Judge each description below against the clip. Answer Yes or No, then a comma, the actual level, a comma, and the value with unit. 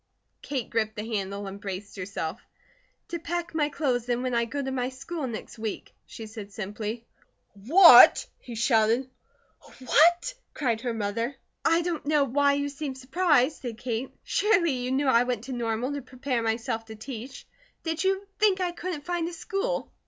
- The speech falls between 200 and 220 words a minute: No, average, 175 wpm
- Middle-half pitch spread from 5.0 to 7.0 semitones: Yes, wide, 5.4 semitones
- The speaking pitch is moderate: No, very high, 255 Hz